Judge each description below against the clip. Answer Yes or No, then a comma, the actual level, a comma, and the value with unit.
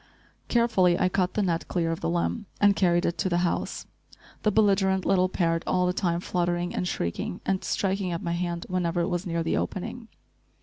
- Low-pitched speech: No, medium, 180 Hz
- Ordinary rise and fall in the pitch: No, narrow, 1.9 semitones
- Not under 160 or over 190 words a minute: No, fast, 205 wpm